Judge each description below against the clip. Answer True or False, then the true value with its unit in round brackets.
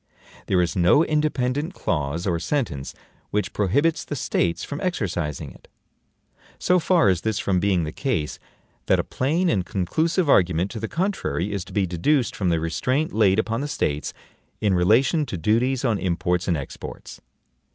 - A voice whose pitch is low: True (105 Hz)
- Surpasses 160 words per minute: True (170 wpm)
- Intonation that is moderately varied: False (8.3 semitones)